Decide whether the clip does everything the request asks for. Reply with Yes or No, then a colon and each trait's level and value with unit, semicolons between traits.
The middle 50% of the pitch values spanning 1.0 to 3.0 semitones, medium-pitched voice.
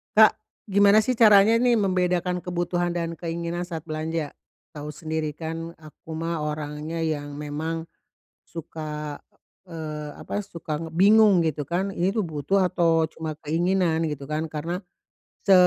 Yes: average, 2.7 semitones; medium, 165 Hz